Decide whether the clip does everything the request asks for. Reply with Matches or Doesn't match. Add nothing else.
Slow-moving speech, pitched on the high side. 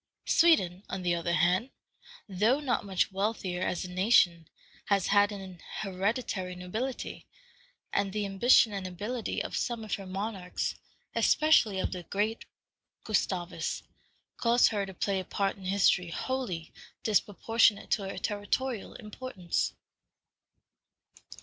Matches